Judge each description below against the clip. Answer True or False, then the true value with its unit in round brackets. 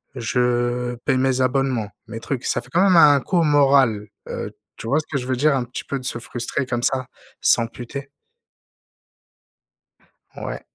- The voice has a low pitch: True (130 Hz)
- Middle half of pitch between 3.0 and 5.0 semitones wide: False (2.4 semitones)